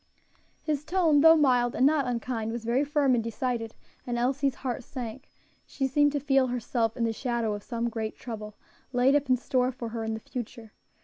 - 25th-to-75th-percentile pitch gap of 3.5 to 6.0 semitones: No, average, 2.9 semitones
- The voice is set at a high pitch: Yes, very high, 250 Hz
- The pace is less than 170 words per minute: No, average, 200 wpm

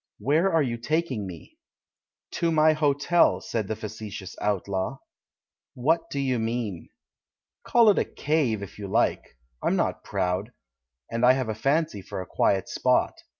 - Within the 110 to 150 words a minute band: No, average, 160 wpm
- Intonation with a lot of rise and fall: Yes, wide, 7.0 semitones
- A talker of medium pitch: No, low, 120 Hz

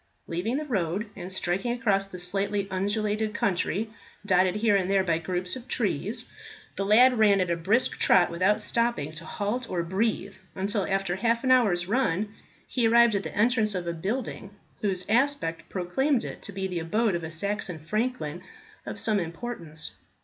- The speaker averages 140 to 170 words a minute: No, average, 180 wpm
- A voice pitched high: Yes, high, 200 Hz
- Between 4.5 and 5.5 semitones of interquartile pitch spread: No, average, 4.1 semitones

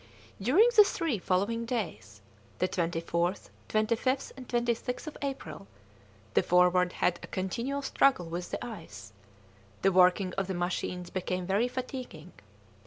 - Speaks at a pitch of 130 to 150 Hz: No, high, 190 Hz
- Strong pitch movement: Yes, wide, 5.7 semitones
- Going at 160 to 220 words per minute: No, slow, 135 wpm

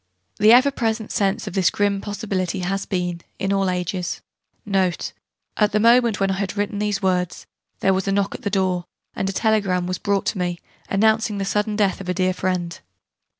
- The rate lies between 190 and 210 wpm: Yes, average, 195 wpm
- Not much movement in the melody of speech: Yes, narrow, 2.1 semitones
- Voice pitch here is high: Yes, high, 195 Hz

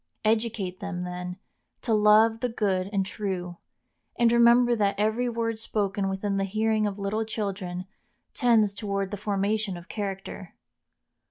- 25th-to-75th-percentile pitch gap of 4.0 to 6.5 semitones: No, narrow, 2.4 semitones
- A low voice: No, high, 205 Hz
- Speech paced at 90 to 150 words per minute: Yes, average, 145 wpm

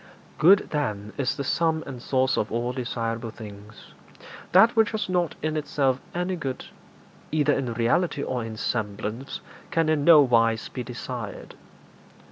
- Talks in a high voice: No, low, 130 Hz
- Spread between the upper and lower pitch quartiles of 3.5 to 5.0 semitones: No, wide, 5.4 semitones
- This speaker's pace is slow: No, average, 150 wpm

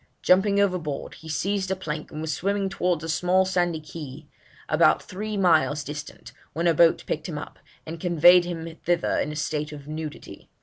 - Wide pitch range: No, average, 3.2 semitones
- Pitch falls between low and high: Yes, medium, 165 Hz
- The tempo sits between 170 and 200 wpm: Yes, average, 190 wpm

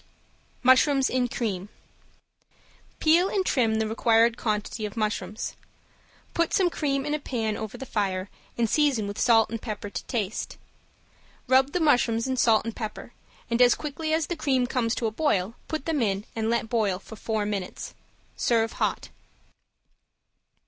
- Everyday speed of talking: Yes, average, 165 wpm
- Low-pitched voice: No, high, 230 Hz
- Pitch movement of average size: Yes, average, 4.0 semitones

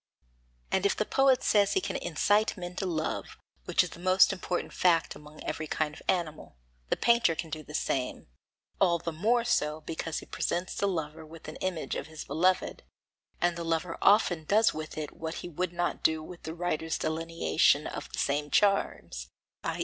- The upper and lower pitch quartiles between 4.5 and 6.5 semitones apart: No, average, 3.0 semitones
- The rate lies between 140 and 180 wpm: No, average, 195 wpm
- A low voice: No, medium, 165 Hz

